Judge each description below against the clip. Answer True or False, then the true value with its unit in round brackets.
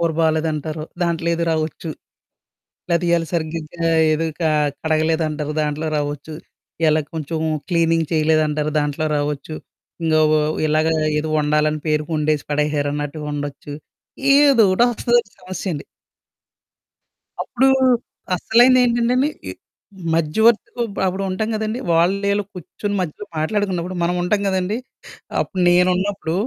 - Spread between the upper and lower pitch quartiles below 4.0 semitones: True (3.5 semitones)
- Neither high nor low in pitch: True (165 Hz)